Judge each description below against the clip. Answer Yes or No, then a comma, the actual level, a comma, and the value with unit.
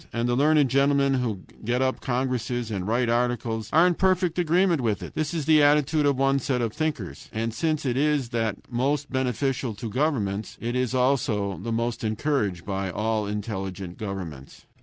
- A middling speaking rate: Yes, average, 180 wpm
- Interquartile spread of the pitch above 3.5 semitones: Yes, average, 4.6 semitones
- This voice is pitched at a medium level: No, low, 125 Hz